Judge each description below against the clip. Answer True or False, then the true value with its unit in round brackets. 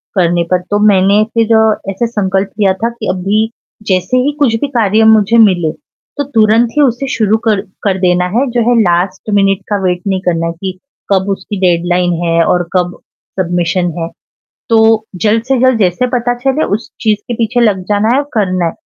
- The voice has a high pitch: True (205 Hz)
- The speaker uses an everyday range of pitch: True (3.9 semitones)